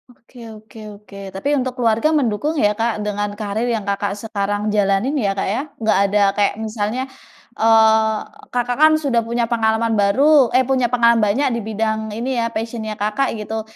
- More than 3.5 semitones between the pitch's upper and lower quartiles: No, average, 2.7 semitones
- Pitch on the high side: Yes, high, 225 Hz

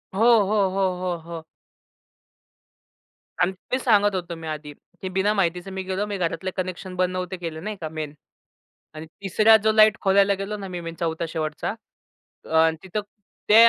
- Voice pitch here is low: No, medium, 185 Hz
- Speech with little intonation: No, average, 3.2 semitones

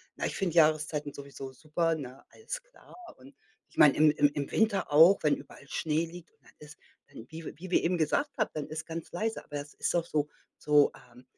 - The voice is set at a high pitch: No, medium, 155 Hz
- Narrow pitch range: No, average, 3.0 semitones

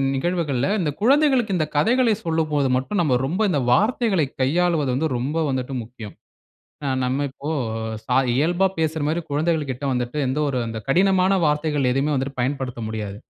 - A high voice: No, medium, 150 Hz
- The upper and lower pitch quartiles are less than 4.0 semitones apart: No, average, 4.9 semitones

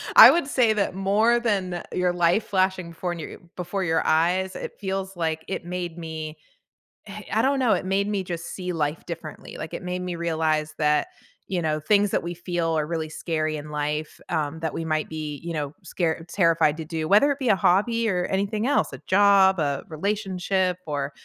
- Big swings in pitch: No, average, 3.6 semitones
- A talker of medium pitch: Yes, medium, 175 Hz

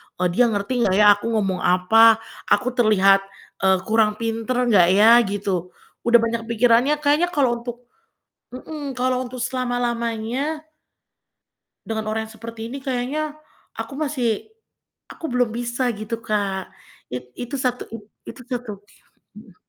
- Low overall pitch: No, high, 230 Hz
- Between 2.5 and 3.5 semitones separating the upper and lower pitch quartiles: Yes, average, 2.9 semitones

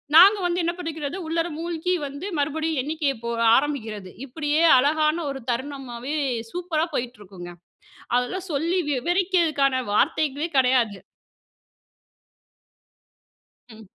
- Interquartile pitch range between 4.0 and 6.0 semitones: Yes, average, 4.6 semitones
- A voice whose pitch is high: Yes, very high, 295 Hz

